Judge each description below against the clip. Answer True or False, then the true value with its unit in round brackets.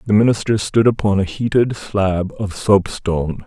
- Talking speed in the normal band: True (175 wpm)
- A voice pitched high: False (100 Hz)